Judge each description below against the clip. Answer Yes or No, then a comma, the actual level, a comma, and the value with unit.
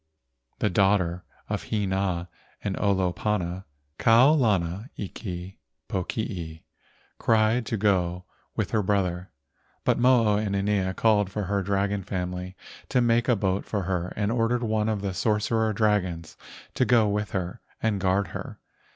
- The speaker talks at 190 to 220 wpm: No, average, 140 wpm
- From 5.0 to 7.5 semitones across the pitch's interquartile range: No, average, 2.9 semitones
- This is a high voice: No, low, 100 Hz